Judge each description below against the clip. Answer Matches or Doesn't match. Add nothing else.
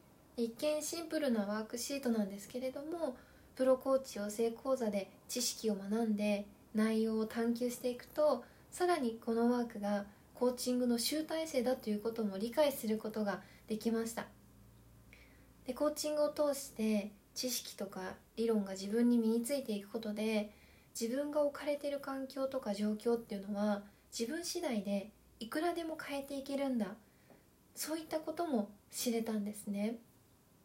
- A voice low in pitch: Doesn't match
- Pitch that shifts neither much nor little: Matches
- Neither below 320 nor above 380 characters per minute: Matches